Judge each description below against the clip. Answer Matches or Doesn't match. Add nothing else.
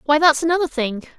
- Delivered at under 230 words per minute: Matches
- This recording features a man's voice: Doesn't match